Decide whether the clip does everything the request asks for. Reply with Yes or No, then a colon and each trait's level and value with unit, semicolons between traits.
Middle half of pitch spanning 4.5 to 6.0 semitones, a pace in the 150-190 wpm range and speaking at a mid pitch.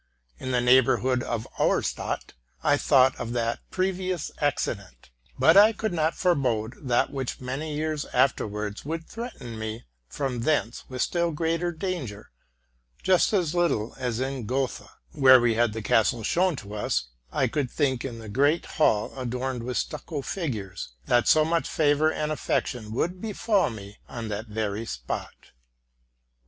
No: wide, 5.6 semitones; average, 155 wpm; low, 130 Hz